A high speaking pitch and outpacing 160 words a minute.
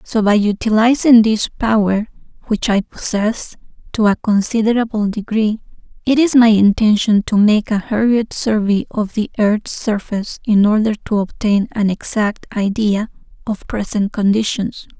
No: high, 215 Hz; average, 140 wpm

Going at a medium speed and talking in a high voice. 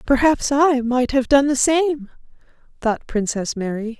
Yes: average, 150 wpm; very high, 260 Hz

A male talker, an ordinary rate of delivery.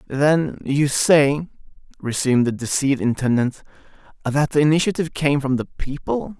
No: male; slow, 130 wpm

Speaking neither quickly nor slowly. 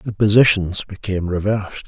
No: slow, 130 wpm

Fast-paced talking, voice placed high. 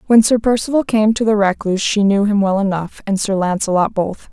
Yes: fast, 220 wpm; high, 205 Hz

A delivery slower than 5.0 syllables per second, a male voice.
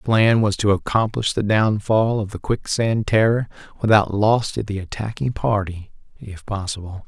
Yes: 4.7 syllables/s; male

